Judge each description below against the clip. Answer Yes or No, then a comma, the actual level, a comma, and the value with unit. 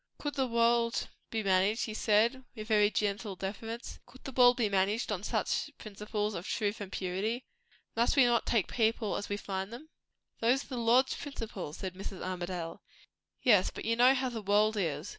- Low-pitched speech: No, high, 215 Hz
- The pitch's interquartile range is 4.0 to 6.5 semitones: No, average, 3.2 semitones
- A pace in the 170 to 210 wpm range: Yes, average, 190 wpm